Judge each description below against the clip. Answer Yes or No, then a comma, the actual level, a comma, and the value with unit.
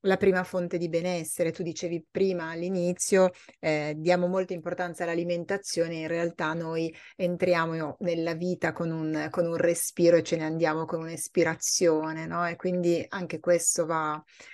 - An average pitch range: No, narrow, 1.5 semitones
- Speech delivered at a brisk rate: No, average, 155 wpm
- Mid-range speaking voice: Yes, medium, 170 Hz